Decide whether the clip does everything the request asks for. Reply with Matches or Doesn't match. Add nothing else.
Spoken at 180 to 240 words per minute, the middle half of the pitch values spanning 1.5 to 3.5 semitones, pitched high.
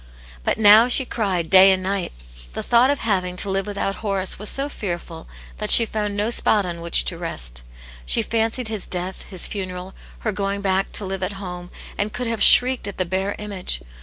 Matches